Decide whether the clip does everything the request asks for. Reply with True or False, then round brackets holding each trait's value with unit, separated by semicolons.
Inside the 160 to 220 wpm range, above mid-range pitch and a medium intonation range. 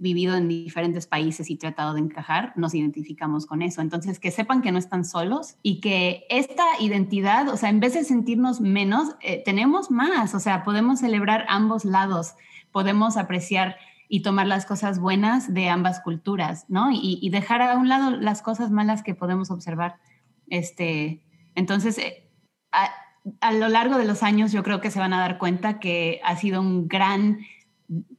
True (180 wpm; 195 Hz; 3.7 semitones)